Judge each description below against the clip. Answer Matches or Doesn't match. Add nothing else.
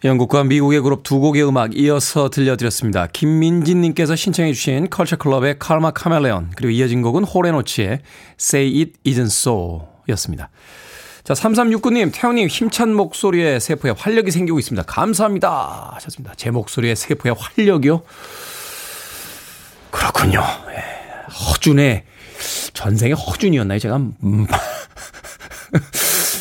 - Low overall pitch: Doesn't match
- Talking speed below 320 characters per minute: Doesn't match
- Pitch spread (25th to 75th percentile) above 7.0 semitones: Doesn't match